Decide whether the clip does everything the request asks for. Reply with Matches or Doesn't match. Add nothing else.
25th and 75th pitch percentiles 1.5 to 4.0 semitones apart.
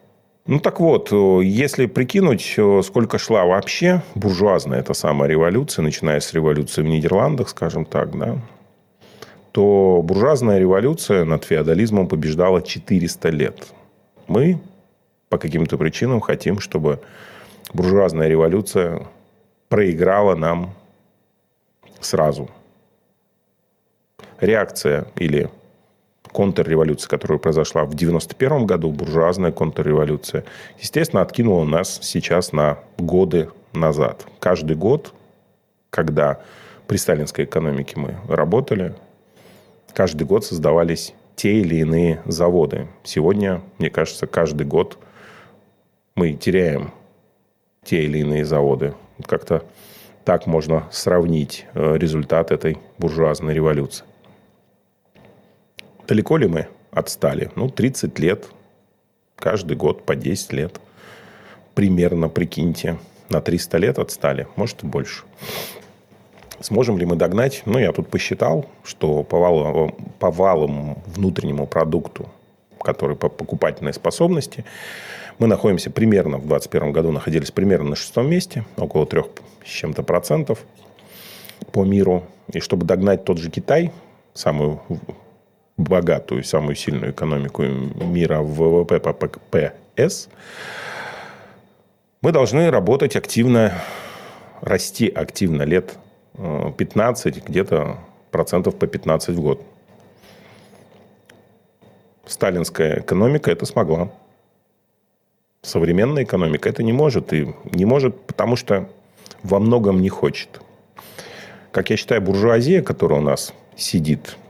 Doesn't match